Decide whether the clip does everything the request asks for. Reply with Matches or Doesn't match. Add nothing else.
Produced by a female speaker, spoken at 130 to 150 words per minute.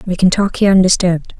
Doesn't match